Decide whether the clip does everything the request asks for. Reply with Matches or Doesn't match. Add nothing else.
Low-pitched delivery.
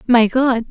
Doesn't match